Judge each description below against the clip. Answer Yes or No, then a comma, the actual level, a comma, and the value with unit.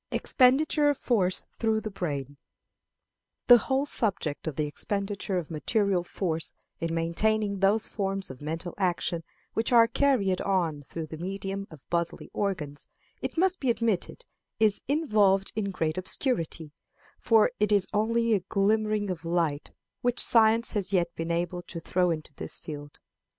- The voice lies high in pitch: Yes, high, 195 Hz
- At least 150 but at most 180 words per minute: Yes, average, 155 wpm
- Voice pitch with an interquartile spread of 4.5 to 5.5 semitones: Yes, average, 4.8 semitones